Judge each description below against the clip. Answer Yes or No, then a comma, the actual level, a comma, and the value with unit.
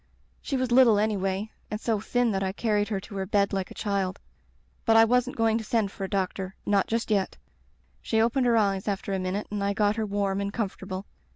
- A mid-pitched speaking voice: No, high, 205 Hz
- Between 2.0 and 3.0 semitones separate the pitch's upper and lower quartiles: Yes, narrow, 2.5 semitones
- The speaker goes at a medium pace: No, fast, 245 wpm